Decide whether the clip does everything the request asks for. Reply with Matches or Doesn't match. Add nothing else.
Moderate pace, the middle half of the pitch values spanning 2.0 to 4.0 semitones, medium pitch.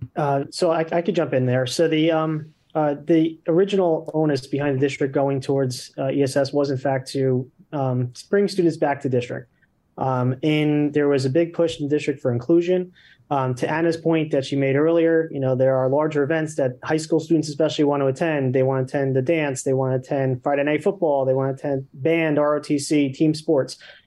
Doesn't match